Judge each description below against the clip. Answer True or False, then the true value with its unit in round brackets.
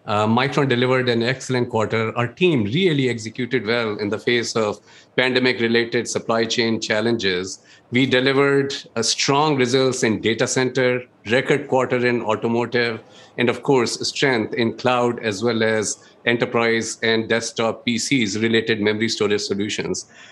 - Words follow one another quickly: False (140 wpm)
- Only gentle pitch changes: True (2.2 semitones)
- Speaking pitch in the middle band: False (120 Hz)